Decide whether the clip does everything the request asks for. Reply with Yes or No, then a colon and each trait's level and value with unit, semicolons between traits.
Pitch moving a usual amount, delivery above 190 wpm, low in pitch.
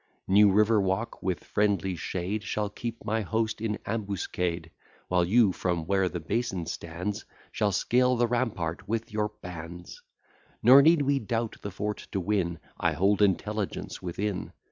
No: average, 3.7 semitones; average, 155 wpm; low, 100 Hz